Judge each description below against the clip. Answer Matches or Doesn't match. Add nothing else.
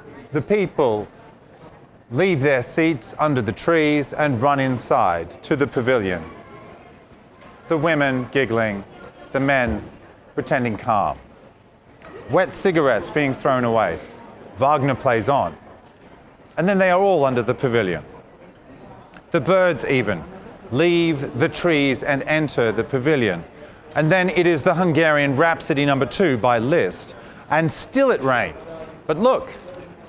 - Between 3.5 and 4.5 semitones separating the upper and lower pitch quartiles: Matches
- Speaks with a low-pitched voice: Doesn't match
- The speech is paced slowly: Matches